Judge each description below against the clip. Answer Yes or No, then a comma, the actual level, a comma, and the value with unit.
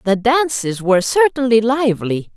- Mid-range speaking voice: No, high, 235 Hz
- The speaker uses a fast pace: No, slow, 125 wpm